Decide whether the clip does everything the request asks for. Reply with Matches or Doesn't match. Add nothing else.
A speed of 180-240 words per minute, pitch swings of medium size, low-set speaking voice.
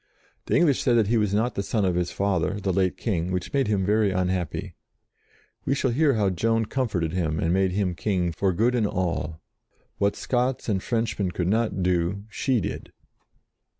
Matches